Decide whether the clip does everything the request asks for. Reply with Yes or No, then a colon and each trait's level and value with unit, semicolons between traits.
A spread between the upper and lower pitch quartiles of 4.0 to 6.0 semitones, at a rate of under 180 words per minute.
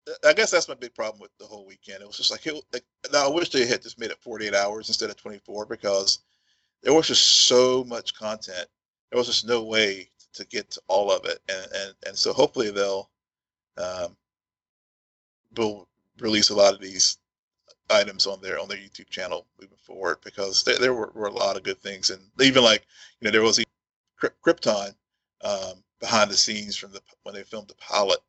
No: average, 4.3 semitones; fast, 205 wpm